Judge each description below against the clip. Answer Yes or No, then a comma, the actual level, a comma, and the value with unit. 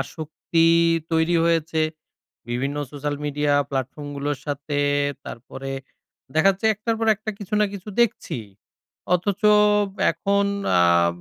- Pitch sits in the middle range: Yes, medium, 150 Hz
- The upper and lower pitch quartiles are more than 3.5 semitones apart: Yes, average, 5.3 semitones